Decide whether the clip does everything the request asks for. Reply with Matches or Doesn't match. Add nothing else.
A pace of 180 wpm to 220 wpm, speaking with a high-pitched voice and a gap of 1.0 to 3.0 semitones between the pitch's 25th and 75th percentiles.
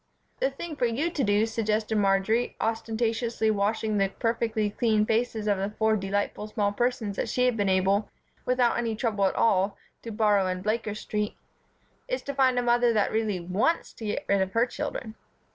Matches